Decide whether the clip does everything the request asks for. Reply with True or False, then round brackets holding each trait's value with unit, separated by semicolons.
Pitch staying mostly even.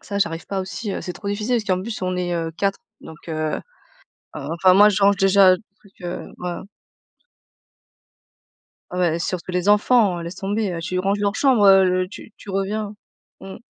True (2.2 semitones)